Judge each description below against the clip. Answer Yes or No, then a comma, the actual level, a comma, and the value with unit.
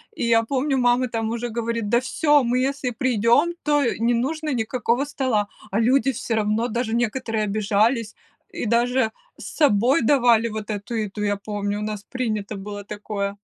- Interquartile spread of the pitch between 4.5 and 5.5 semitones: No, average, 3.2 semitones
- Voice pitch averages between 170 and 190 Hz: No, high, 230 Hz